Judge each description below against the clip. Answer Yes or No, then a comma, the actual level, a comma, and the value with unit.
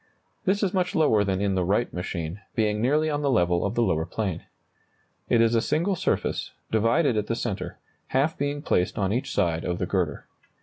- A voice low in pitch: Yes, low, 110 Hz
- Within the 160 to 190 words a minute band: No, fast, 205 wpm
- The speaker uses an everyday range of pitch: No, wide, 7.2 semitones